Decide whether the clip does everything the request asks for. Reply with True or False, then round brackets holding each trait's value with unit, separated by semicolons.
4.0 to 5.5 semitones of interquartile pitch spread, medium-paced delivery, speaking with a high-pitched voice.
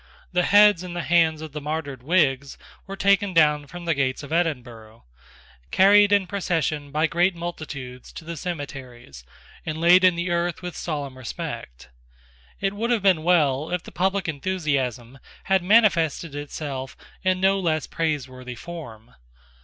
False (4.5 semitones; 155 wpm; 160 Hz)